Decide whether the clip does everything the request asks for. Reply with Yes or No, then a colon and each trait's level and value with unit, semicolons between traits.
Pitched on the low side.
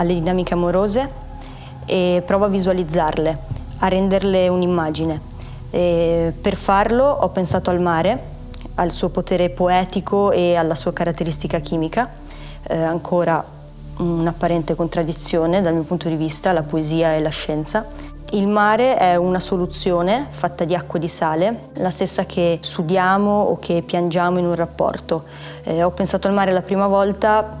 No: medium, 175 Hz